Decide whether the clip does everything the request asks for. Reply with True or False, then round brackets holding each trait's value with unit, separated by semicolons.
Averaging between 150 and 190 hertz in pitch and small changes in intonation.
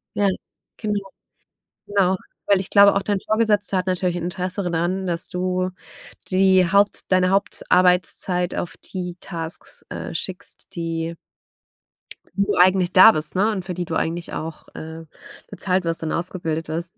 True (185 Hz; 2.3 semitones)